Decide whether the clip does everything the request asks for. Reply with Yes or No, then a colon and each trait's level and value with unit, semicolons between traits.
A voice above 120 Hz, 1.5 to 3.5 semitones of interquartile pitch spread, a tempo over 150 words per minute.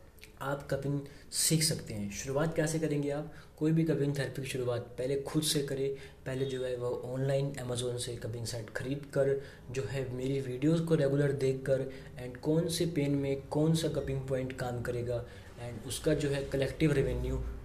Yes: low, 135 Hz; narrow, 2.4 semitones; average, 185 wpm